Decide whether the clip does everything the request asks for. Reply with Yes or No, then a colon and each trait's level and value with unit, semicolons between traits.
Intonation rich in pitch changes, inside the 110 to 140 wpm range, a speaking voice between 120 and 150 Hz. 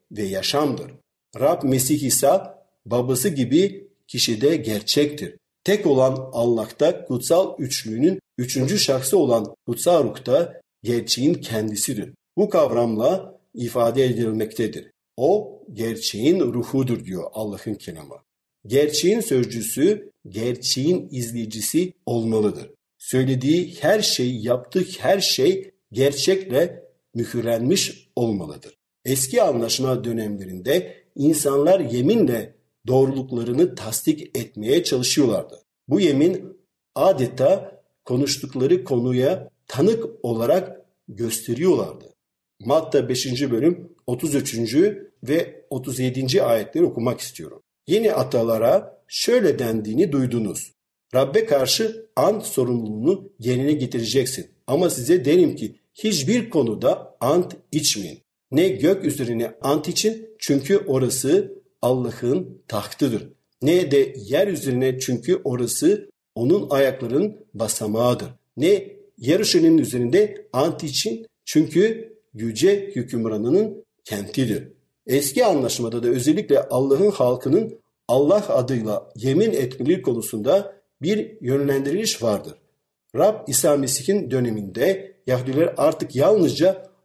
No: wide, 7.8 semitones; slow, 95 wpm; low, 135 Hz